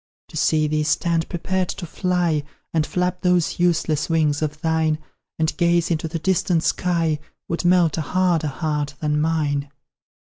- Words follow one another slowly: No, average, 155 wpm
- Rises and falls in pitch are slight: Yes, narrow, 2.3 semitones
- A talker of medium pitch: Yes, medium, 160 Hz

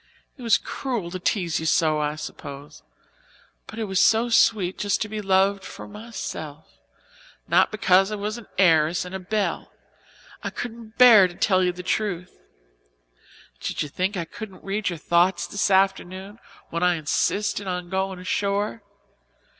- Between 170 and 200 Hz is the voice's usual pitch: Yes, high, 190 Hz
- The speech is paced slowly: No, average, 160 wpm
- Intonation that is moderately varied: Yes, average, 3.1 semitones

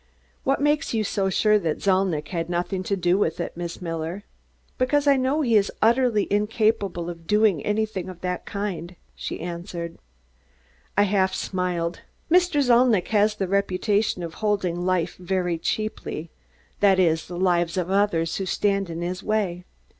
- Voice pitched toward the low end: No, high, 190 Hz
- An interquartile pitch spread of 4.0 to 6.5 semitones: No, average, 3.4 semitones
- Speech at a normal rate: Yes, average, 160 wpm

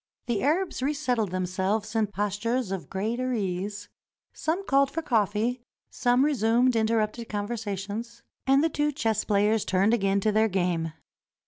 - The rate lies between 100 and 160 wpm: Yes, average, 140 wpm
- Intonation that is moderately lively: Yes, average, 3.7 semitones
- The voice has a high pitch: Yes, high, 220 Hz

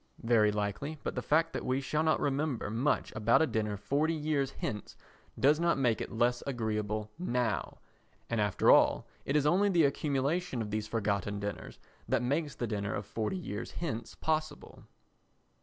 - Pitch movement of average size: No, wide, 6.0 semitones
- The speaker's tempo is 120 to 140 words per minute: No, average, 175 wpm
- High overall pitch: No, low, 125 Hz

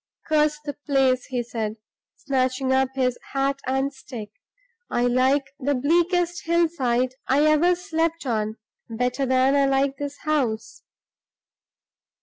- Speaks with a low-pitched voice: No, very high, 270 Hz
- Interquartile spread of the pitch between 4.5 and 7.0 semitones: No, average, 3.0 semitones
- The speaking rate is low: Yes, slow, 130 wpm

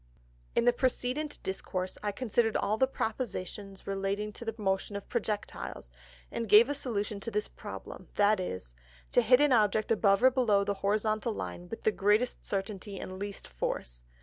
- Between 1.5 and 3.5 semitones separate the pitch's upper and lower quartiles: Yes, average, 2.9 semitones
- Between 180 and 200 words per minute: No, average, 170 wpm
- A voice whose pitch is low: No, high, 210 Hz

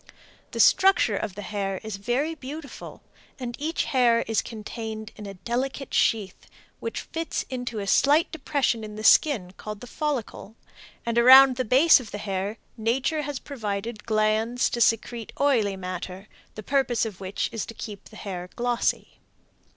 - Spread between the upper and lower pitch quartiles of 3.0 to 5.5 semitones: Yes, average, 4.1 semitones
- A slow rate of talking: No, average, 165 wpm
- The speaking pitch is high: Yes, high, 230 Hz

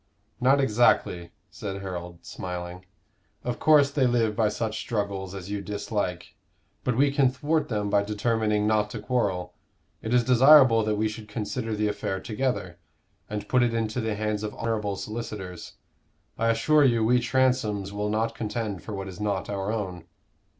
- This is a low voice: Yes, low, 110 Hz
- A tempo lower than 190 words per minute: Yes, average, 170 wpm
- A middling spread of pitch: Yes, average, 3.1 semitones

